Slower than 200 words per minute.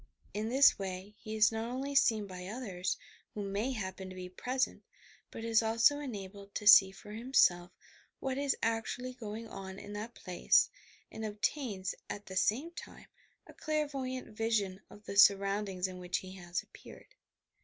Yes: average, 165 wpm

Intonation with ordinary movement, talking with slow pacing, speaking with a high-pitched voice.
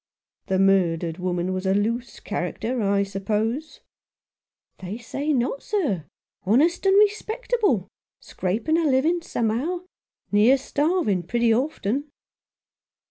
No: wide, 8.0 semitones; slow, 130 wpm; high, 230 Hz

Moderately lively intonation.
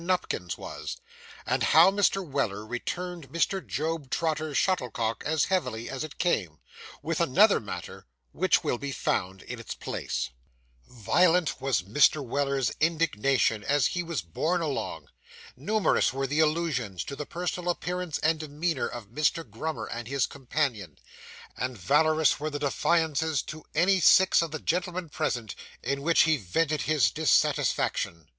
Yes: average, 4.9 semitones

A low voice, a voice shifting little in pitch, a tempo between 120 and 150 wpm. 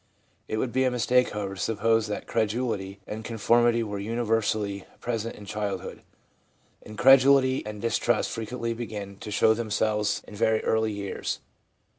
Yes: low, 110 Hz; narrow, 2.2 semitones; average, 145 wpm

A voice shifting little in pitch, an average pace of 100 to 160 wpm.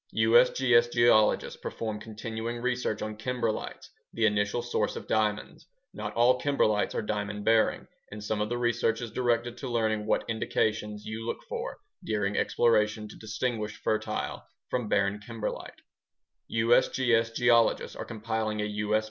Yes: narrow, 1.9 semitones; average, 145 wpm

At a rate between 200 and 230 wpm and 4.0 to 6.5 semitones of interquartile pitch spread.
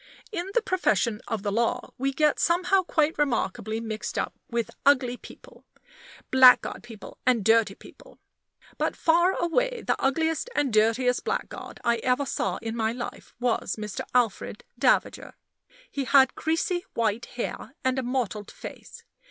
No: average, 150 wpm; average, 5.2 semitones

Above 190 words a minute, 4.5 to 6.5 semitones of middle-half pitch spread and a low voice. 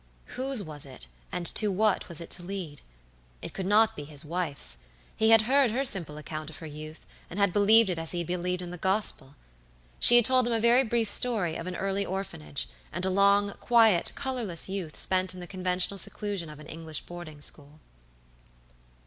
No: average, 200 wpm; average, 5.0 semitones; medium, 185 Hz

